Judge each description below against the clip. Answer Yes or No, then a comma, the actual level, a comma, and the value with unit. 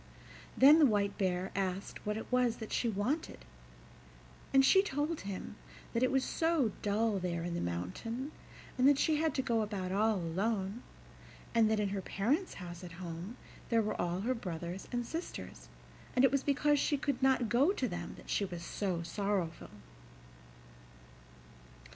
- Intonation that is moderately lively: No, wide, 6.2 semitones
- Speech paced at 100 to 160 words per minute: No, average, 170 wpm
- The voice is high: Yes, high, 215 Hz